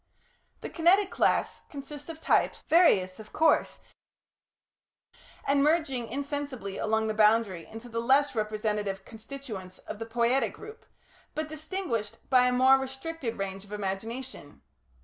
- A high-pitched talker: Yes, high, 240 Hz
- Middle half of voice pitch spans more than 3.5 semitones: Yes, average, 5.1 semitones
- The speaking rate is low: Yes, slow, 130 wpm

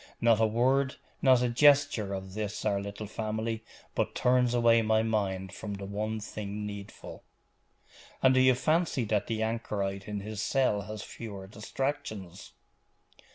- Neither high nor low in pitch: No, low, 110 Hz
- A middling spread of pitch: Yes, average, 3.2 semitones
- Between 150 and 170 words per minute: Yes, average, 155 wpm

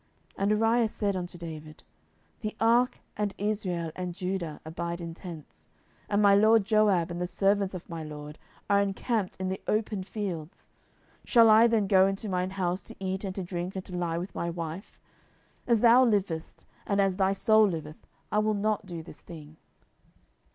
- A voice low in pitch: No, high, 190 Hz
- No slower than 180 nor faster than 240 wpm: Yes, average, 185 wpm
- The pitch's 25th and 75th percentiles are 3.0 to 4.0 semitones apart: Yes, average, 3.5 semitones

